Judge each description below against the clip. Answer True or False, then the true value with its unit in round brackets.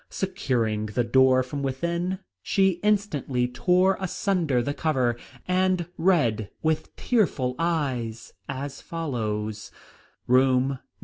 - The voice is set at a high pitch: False (140 Hz)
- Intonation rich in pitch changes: True (6.4 semitones)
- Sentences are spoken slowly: True (110 wpm)